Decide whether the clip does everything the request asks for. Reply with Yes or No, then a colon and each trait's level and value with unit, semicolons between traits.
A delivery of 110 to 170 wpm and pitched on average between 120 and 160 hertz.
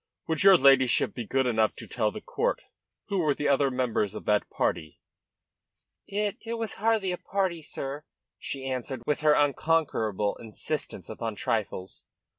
Yes: average, 160 wpm; medium, 140 Hz